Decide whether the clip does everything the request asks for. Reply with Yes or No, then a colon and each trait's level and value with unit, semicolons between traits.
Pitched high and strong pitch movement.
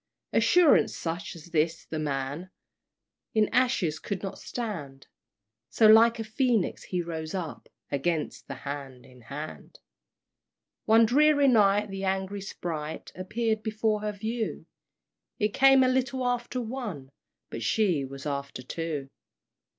Yes: high, 195 Hz; wide, 6.9 semitones